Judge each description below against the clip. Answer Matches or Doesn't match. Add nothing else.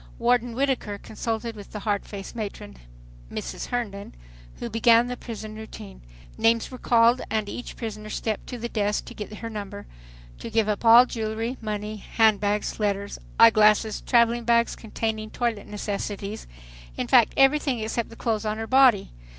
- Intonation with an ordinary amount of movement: Doesn't match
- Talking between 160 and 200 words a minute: Matches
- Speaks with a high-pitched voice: Matches